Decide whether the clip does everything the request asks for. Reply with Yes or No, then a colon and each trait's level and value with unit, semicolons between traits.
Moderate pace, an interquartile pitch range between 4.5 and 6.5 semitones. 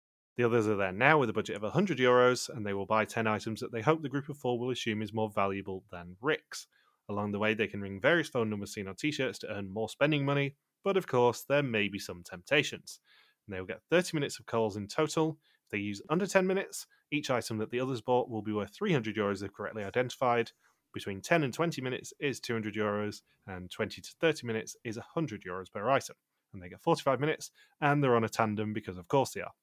No: fast, 245 wpm; wide, 5.4 semitones